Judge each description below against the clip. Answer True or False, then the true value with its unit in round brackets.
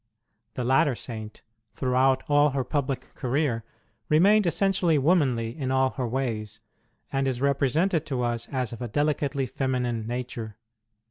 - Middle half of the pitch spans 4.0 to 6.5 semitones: False (3.2 semitones)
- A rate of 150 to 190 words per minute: False (140 wpm)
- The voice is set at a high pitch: False (130 Hz)